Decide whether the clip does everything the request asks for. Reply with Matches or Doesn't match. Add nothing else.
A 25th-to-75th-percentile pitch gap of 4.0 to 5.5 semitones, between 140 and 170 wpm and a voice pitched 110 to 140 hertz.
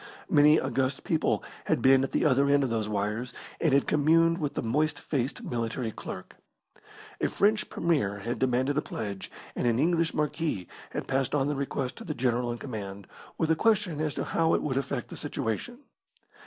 Doesn't match